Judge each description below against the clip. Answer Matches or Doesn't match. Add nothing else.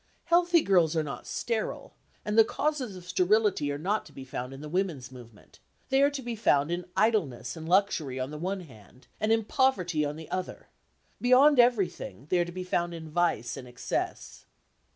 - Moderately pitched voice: Matches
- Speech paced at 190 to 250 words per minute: Matches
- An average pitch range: Doesn't match